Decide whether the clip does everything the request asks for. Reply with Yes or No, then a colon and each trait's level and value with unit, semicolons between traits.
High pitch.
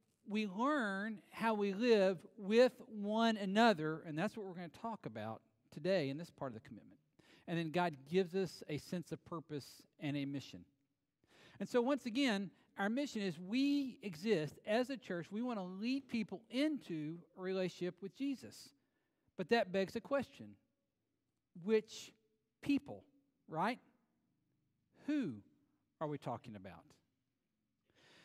Yes: high, 195 Hz